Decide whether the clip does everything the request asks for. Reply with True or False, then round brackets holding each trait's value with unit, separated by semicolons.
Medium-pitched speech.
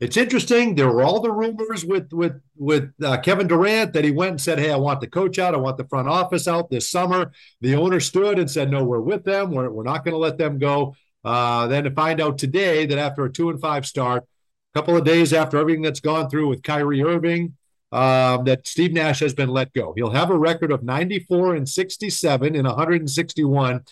True (155 Hz)